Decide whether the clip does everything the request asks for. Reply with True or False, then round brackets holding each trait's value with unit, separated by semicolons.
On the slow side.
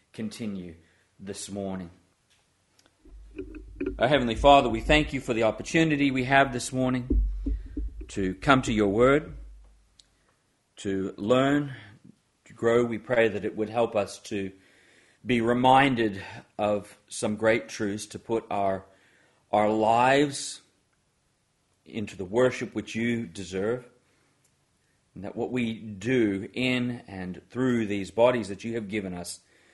True (130 wpm)